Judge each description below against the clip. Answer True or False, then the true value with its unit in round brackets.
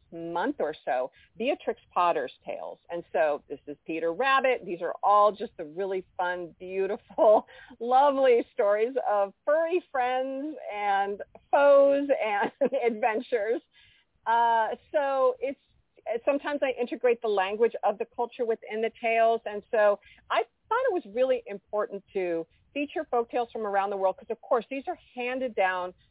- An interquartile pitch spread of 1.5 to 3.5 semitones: False (5.3 semitones)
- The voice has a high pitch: True (230 Hz)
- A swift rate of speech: False (150 wpm)